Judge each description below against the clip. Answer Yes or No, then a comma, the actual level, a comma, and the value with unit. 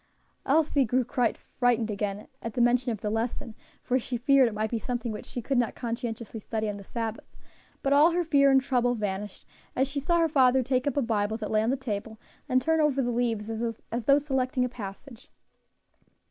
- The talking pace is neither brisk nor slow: No, fast, 210 wpm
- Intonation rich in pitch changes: No, average, 3.3 semitones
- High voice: Yes, high, 245 Hz